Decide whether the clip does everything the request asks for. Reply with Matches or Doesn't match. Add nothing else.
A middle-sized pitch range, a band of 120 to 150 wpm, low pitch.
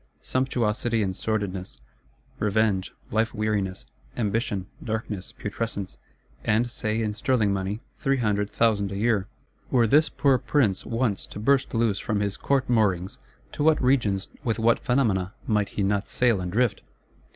Matches